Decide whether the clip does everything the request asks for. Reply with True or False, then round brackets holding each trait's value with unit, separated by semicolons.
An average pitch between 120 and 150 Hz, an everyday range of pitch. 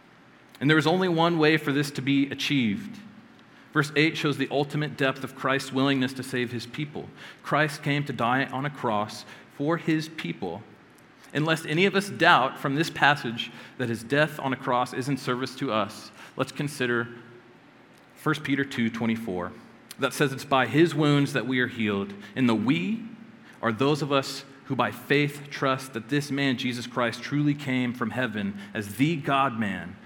True (135 Hz; 3.4 semitones)